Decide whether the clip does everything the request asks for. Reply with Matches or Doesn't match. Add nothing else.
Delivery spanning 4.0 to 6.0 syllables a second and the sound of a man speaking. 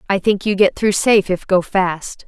Doesn't match